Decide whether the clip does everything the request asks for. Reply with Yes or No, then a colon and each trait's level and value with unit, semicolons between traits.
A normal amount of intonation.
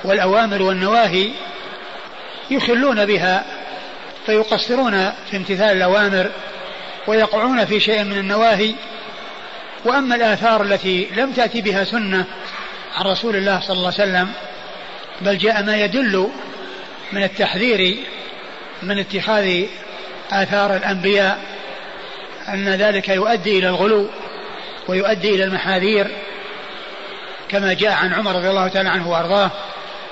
No: narrow, 2.0 semitones